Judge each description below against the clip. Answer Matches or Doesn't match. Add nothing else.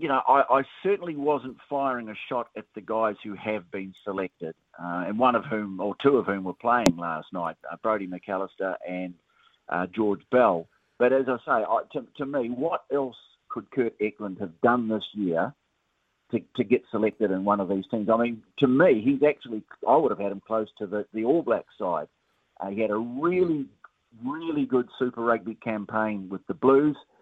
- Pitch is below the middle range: Matches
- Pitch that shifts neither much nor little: Matches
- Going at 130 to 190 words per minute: Doesn't match